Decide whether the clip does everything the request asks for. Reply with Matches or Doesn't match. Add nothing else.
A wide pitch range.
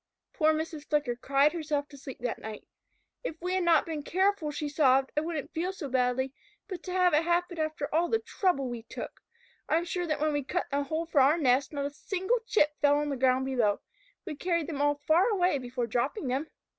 Doesn't match